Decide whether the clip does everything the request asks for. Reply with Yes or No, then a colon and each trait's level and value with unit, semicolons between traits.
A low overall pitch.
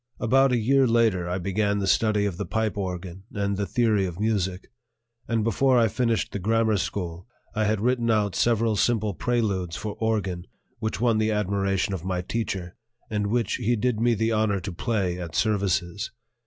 Yes: low, 105 Hz